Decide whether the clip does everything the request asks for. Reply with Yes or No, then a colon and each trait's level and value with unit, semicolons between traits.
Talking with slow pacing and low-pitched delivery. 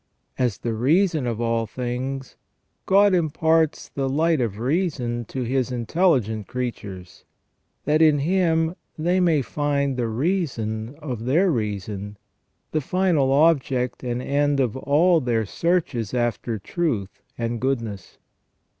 Yes: slow, 130 wpm; low, 130 Hz